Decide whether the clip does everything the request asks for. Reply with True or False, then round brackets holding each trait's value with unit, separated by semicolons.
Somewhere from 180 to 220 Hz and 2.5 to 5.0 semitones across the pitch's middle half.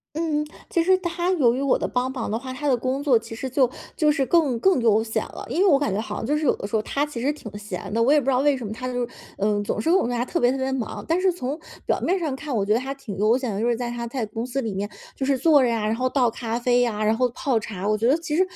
False (255 Hz; 4.2 semitones)